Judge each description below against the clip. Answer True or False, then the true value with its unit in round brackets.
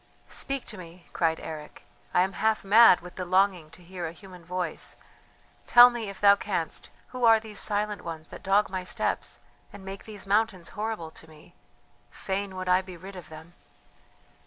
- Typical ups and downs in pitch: True (3.2 semitones)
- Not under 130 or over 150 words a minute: False (185 wpm)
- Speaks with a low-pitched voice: False (190 Hz)